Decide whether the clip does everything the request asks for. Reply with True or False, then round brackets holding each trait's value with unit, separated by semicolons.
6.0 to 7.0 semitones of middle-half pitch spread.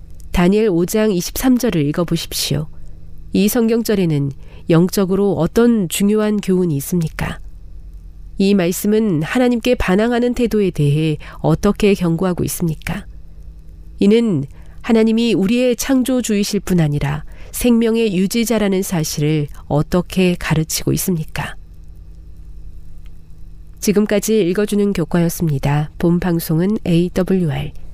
True (6.4 semitones)